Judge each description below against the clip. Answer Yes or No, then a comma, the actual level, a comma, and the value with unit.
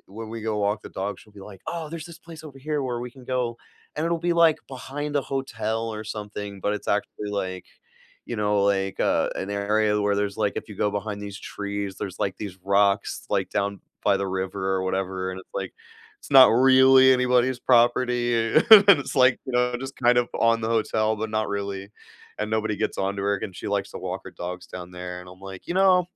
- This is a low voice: Yes, low, 105 Hz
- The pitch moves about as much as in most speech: Yes, average, 4.2 semitones